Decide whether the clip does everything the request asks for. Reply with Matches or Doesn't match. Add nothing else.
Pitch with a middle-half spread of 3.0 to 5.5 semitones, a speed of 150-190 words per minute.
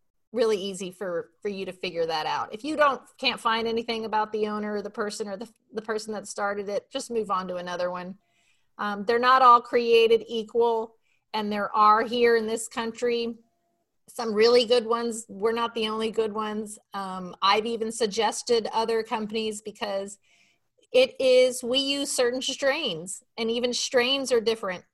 Doesn't match